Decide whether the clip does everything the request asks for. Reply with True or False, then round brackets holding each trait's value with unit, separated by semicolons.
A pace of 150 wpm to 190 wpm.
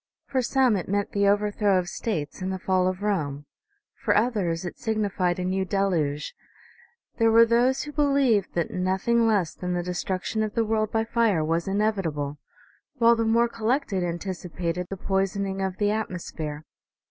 True (170 wpm)